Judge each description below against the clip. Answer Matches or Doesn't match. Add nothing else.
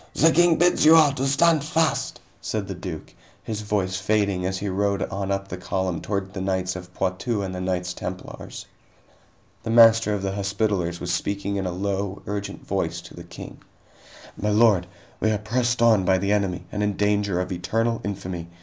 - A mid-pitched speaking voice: Doesn't match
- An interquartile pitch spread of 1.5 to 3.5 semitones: Matches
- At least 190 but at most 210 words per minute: Matches